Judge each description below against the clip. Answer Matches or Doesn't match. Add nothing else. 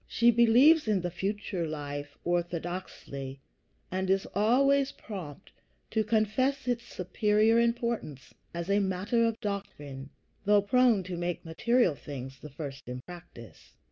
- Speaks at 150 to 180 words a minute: Doesn't match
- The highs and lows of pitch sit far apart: Matches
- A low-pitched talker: Doesn't match